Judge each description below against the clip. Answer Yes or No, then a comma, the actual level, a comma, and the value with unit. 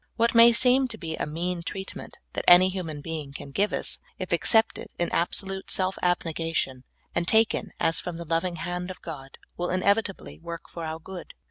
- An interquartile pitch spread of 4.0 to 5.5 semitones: No, average, 2.8 semitones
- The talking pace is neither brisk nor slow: Yes, average, 195 wpm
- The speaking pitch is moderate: Yes, medium, 175 Hz